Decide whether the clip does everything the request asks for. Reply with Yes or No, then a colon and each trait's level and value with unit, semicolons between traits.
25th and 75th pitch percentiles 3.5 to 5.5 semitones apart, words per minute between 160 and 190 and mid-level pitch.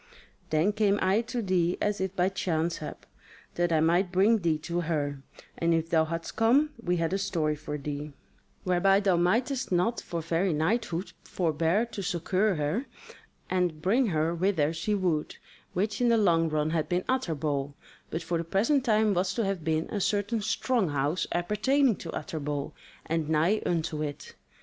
Yes: average, 4.3 semitones; average, 180 wpm; medium, 175 Hz